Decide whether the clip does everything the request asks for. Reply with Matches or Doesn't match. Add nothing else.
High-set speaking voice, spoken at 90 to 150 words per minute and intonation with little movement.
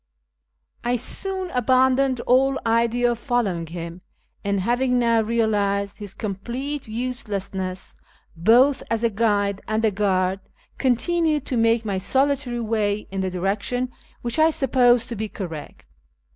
Doesn't match